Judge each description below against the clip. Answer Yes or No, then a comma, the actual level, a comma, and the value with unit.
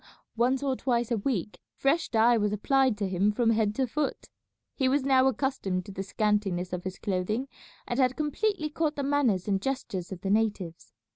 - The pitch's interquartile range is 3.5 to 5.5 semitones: Yes, average, 5.2 semitones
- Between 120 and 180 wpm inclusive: No, average, 195 wpm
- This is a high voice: Yes, high, 230 Hz